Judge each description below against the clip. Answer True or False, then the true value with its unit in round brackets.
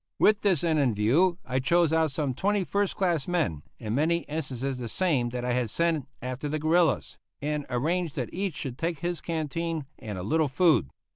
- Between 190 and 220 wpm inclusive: True (200 wpm)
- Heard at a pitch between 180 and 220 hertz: False (155 Hz)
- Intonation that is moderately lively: True (4.9 semitones)